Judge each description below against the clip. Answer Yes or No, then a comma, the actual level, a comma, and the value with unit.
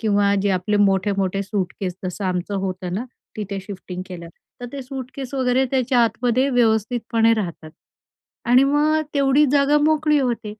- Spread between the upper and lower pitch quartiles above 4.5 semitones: Yes, average, 5.3 semitones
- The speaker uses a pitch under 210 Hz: No, high, 225 Hz